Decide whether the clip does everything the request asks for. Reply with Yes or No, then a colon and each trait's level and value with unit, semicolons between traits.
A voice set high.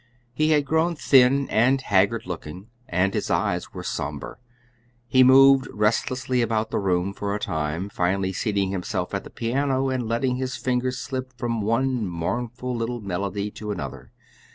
No: low, 115 Hz